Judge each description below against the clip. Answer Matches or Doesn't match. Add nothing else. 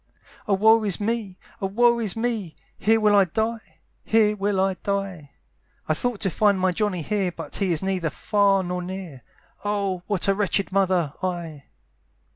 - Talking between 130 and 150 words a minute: Doesn't match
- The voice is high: Matches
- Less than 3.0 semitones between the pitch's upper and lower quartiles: Matches